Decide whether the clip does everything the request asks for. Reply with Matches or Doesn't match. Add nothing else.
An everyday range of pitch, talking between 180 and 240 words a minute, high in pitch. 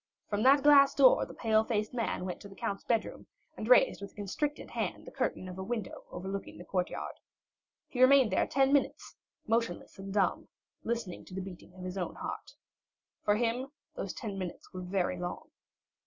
Matches